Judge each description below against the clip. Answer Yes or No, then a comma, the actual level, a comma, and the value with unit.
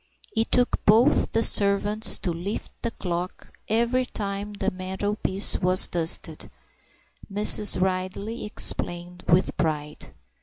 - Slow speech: Yes, slow, 115 wpm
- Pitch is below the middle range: No, high, 200 Hz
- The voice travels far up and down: No, average, 2.9 semitones